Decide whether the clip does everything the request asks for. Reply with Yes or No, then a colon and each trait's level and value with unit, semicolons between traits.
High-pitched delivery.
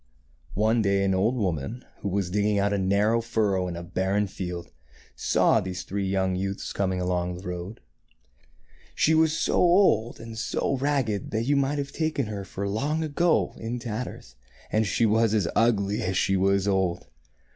No: low, 100 Hz